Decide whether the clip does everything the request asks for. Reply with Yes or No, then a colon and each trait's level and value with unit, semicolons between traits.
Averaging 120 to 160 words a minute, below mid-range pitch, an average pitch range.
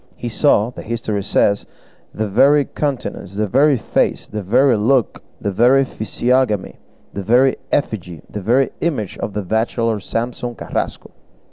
Yes: average, 145 wpm; low, 115 Hz; average, 3.9 semitones